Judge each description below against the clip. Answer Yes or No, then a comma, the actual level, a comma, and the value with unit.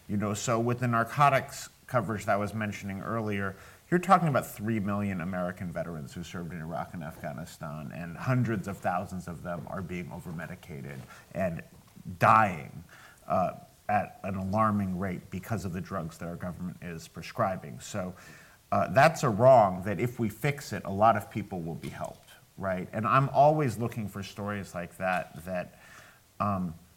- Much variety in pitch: No, average, 3.9 semitones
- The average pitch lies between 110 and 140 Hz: No, low, 100 Hz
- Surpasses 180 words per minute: No, average, 175 wpm